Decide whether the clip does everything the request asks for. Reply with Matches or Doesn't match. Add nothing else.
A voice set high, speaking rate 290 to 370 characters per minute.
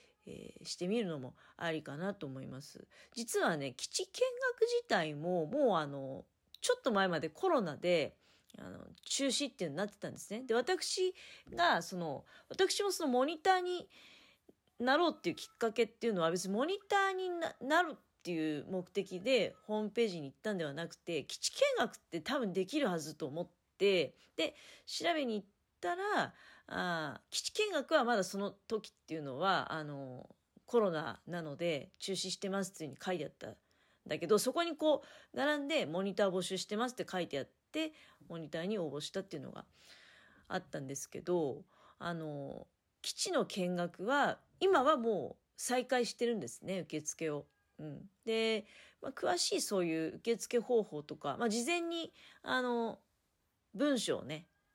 Matches